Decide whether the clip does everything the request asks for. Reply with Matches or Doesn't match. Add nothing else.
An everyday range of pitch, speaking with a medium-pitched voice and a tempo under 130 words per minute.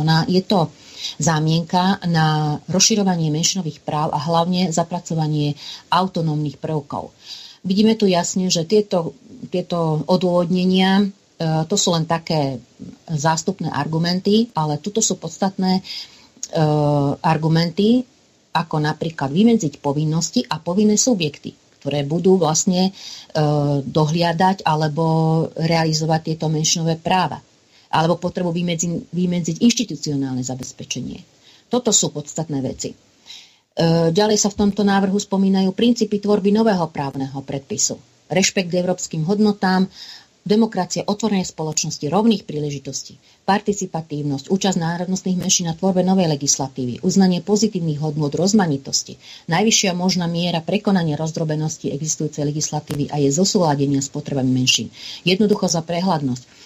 Matches